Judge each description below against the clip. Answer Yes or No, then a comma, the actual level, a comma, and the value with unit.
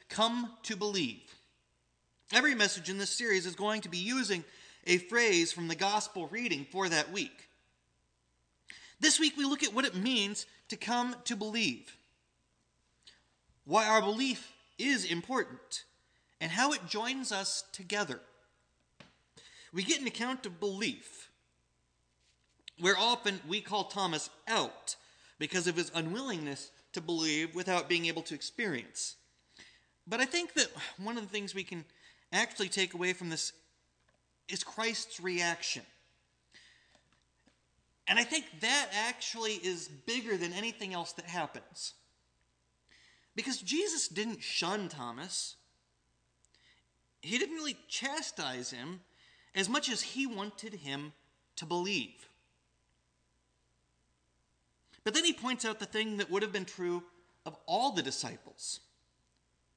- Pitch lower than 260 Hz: Yes, high, 190 Hz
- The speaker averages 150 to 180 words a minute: No, slow, 135 wpm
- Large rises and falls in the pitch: Yes, wide, 6.7 semitones